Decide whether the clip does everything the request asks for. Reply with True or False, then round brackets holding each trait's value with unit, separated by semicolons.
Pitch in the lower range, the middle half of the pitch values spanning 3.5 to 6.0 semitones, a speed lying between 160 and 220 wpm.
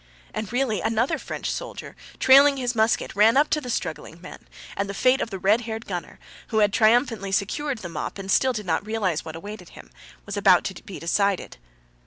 False (215 Hz; 3.9 semitones; 205 wpm)